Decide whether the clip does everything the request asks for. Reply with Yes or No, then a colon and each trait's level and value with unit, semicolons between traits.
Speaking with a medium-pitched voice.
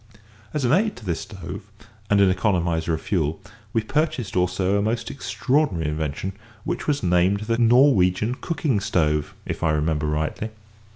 No: very low, 95 Hz